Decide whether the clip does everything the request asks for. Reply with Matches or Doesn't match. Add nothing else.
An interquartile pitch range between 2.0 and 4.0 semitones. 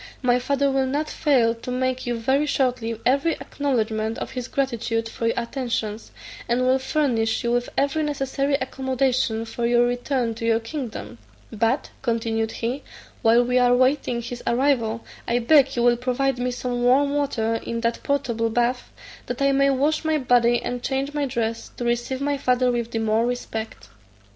Matches